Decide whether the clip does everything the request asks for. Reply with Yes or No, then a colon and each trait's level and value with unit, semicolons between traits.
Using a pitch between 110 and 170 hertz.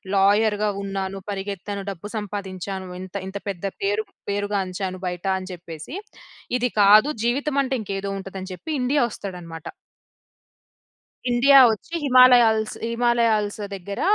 No: high, 200 Hz